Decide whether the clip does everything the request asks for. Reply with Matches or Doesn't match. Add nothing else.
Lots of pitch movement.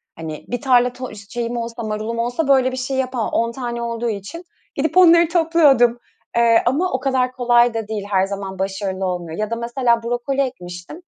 Doesn't match